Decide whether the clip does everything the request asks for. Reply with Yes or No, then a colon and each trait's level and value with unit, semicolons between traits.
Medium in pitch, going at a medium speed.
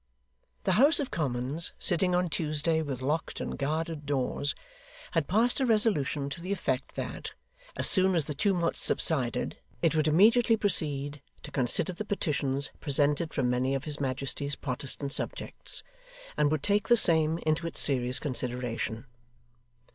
Yes: medium, 155 Hz; average, 155 wpm